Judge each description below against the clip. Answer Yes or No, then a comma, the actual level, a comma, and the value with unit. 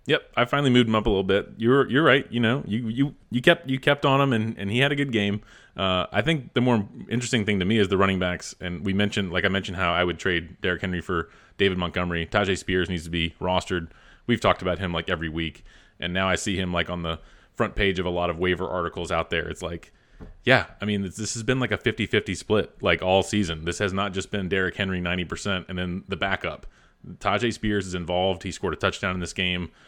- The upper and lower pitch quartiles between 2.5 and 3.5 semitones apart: Yes, average, 3.2 semitones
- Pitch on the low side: Yes, very low, 95 Hz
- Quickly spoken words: Yes, fast, 255 wpm